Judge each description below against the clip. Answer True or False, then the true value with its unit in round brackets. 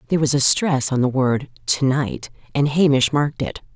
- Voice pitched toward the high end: False (140 Hz)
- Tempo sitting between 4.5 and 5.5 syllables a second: True (5.2 syllables/s)